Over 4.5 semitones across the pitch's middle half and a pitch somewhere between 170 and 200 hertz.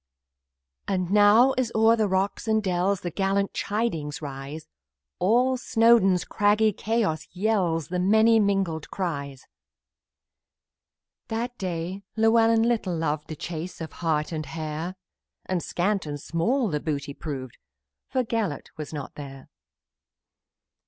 Yes: wide, 5.6 semitones; medium, 185 Hz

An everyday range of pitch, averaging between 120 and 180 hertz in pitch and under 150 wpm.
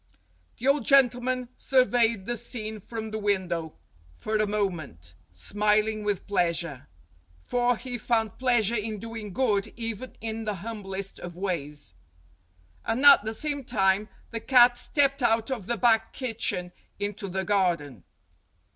No: average, 3.8 semitones; high, 215 Hz; average, 140 wpm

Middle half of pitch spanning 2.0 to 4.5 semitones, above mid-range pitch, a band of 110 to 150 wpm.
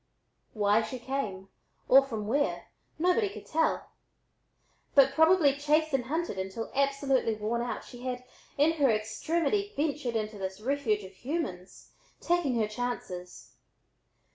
No: wide, 5.6 semitones; very high, 255 Hz; slow, 135 wpm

